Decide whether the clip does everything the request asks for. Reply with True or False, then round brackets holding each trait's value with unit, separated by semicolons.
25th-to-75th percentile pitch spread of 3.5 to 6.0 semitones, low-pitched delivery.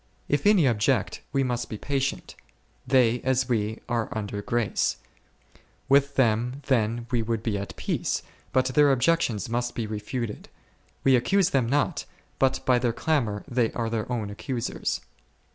False (3.0 semitones; 120 Hz)